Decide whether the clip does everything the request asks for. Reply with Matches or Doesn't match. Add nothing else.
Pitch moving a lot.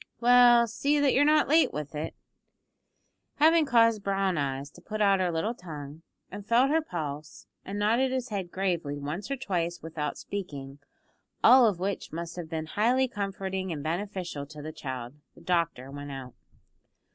Matches